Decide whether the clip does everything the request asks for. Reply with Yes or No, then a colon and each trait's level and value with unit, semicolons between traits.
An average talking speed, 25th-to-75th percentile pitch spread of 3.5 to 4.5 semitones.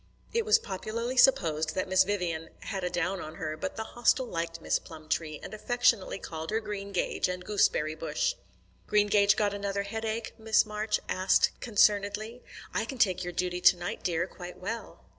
Yes: average, 175 wpm; average, 3.8 semitones